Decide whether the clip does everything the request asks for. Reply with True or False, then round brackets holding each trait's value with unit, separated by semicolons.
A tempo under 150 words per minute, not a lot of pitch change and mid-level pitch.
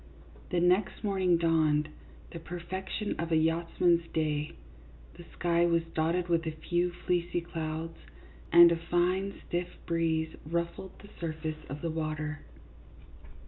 True (140 wpm; 1.6 semitones; 170 Hz)